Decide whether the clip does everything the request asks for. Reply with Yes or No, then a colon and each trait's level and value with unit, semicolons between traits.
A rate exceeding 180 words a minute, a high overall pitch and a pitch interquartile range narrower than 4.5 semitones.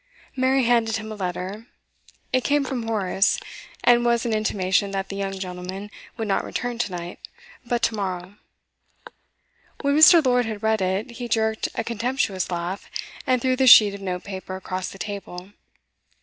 No: average, 170 wpm; high, 215 Hz; average, 4.0 semitones